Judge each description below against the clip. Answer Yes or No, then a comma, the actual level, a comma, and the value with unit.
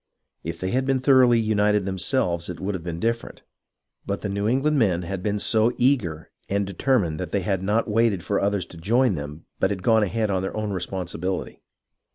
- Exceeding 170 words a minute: Yes, fast, 205 wpm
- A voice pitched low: Yes, low, 100 Hz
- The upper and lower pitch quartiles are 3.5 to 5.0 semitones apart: Yes, average, 3.9 semitones